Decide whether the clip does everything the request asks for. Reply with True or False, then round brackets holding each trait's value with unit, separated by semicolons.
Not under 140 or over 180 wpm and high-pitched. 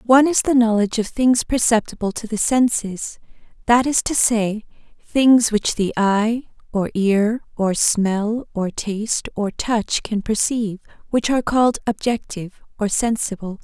True (145 wpm; 220 Hz)